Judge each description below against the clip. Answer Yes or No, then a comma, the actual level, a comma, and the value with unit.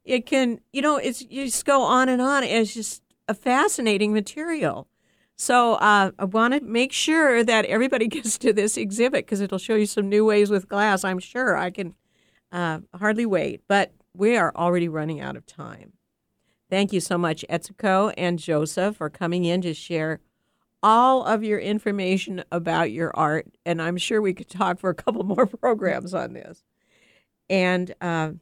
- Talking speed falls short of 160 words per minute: No, average, 185 wpm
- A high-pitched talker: Yes, high, 205 Hz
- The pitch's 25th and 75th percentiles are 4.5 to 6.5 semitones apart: Yes, average, 4.9 semitones